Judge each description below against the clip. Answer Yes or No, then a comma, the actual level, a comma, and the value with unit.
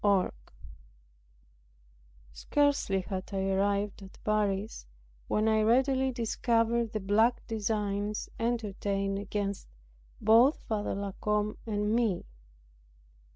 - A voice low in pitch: No, high, 210 Hz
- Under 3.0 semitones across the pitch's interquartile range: Yes, narrow, 2.4 semitones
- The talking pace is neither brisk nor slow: No, slow, 105 wpm